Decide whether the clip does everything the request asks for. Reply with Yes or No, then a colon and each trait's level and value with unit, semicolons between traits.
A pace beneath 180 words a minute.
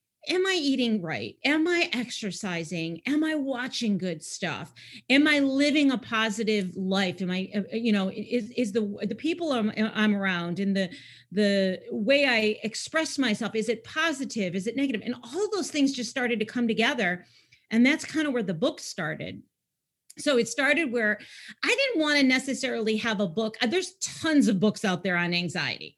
No: average, 185 wpm